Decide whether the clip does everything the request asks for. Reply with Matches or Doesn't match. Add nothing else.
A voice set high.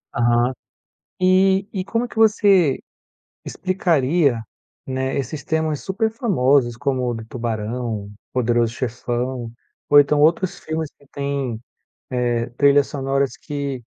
Doesn't match